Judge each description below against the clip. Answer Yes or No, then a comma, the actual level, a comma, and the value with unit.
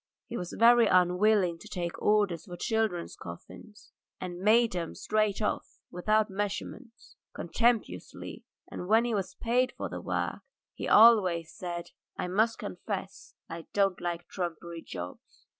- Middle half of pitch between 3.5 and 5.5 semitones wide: Yes, average, 3.9 semitones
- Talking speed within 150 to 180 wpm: No, average, 140 wpm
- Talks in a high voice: Yes, high, 195 Hz